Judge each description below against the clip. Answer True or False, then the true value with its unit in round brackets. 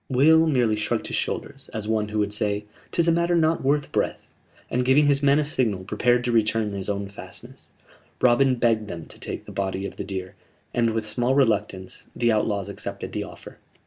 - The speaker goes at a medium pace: False (210 wpm)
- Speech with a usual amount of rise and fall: True (4.7 semitones)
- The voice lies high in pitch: False (115 Hz)